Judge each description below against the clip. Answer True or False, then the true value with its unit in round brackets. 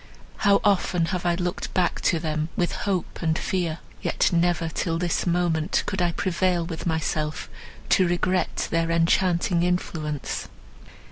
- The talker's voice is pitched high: False (175 Hz)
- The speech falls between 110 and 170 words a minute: True (140 wpm)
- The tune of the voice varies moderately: False (1.5 semitones)